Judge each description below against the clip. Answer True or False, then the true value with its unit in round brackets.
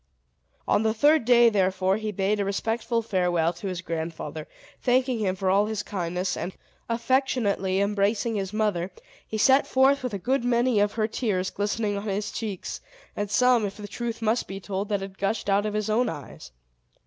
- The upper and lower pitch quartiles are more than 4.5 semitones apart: False (3.1 semitones)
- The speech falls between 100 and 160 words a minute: False (195 wpm)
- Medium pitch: False (210 Hz)